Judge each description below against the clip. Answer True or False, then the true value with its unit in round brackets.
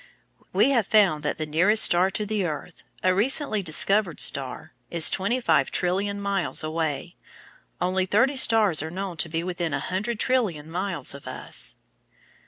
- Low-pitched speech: False (185 Hz)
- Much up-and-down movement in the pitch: False (4.5 semitones)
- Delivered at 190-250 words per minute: False (165 wpm)